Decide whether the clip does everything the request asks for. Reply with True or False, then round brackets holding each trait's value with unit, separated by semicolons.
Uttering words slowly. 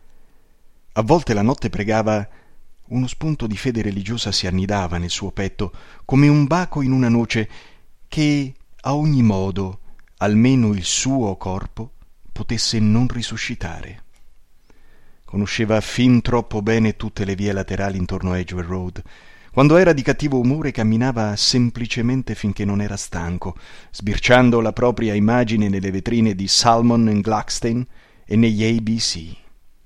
False (135 wpm)